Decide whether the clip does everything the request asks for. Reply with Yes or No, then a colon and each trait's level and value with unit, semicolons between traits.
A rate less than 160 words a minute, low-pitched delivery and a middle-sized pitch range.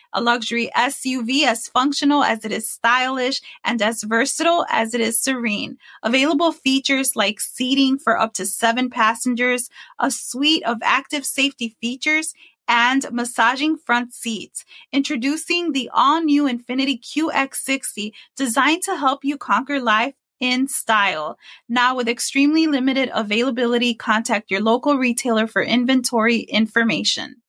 No: slow, 135 wpm; very high, 255 Hz; average, 3.1 semitones